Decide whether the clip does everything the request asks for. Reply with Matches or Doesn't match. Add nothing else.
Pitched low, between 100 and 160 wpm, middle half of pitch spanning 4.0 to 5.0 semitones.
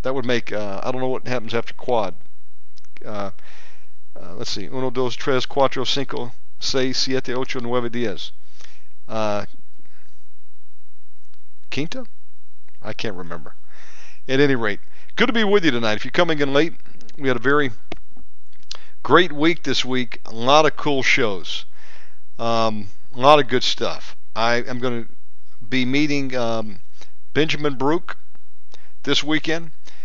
Matches